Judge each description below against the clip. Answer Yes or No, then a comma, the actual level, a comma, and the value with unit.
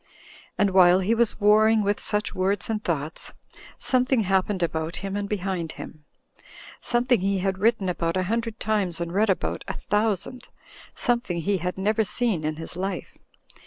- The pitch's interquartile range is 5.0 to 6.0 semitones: No, average, 3.3 semitones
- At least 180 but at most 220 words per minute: No, average, 165 wpm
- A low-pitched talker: No, high, 195 Hz